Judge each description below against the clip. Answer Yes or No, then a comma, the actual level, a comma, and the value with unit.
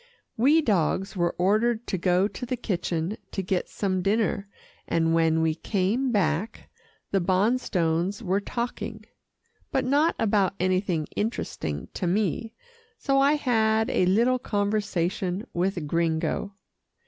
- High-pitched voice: Yes, high, 195 Hz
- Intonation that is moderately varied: Yes, average, 4.1 semitones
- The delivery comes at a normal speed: No, slow, 130 wpm